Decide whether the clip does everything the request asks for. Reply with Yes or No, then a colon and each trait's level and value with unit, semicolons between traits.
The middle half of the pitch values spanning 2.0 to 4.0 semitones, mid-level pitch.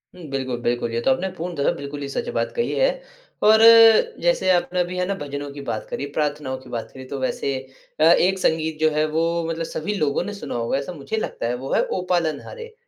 No: average, 4.9 semitones; medium, 155 Hz